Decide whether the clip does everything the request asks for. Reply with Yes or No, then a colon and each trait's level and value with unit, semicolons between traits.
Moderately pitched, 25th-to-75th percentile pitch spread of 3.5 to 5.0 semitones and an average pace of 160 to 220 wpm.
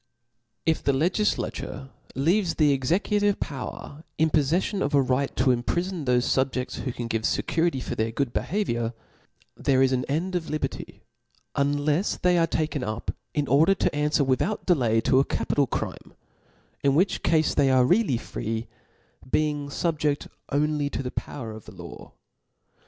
Yes: medium, 145 Hz; average, 4.1 semitones; average, 165 wpm